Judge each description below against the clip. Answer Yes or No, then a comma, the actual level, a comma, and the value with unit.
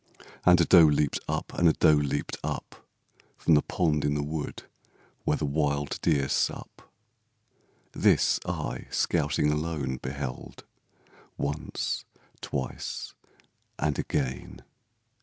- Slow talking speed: Yes, slow, 120 wpm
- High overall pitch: No, very low, 75 Hz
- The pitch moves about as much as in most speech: No, narrow, 1.7 semitones